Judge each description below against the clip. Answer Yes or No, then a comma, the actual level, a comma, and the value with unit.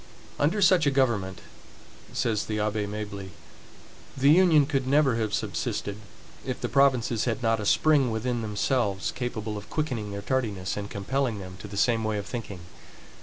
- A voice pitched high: No, low, 115 Hz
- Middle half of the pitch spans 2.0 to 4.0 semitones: No, average, 4.5 semitones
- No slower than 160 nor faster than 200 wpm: Yes, average, 170 wpm